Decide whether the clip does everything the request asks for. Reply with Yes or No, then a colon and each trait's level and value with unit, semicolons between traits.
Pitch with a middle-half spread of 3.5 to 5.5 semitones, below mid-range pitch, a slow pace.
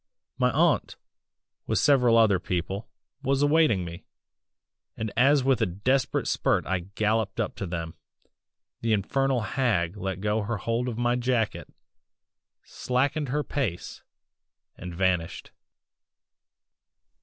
Yes: average, 5.2 semitones; low, 110 Hz; slow, 120 wpm